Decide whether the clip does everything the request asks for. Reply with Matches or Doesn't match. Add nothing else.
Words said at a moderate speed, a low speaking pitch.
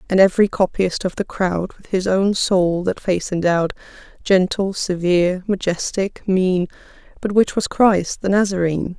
Doesn't match